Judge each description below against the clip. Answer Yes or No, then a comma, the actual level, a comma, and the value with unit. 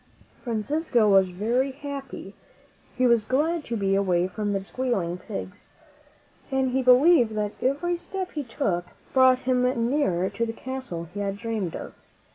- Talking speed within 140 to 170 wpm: Yes, average, 160 wpm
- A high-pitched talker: Yes, high, 235 Hz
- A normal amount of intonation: Yes, average, 5.0 semitones